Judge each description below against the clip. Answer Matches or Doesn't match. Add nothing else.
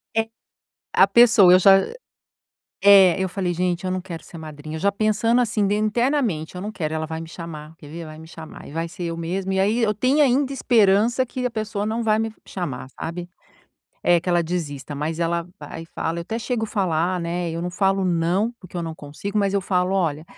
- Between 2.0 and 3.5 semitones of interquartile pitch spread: Doesn't match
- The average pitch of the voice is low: Doesn't match